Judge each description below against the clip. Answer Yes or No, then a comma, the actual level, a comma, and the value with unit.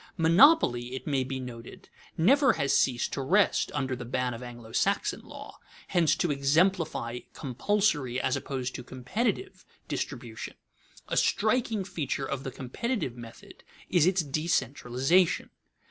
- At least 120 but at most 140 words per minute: Yes, slow, 135 wpm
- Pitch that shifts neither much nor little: No, wide, 6.7 semitones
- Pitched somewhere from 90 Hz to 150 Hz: Yes, medium, 140 Hz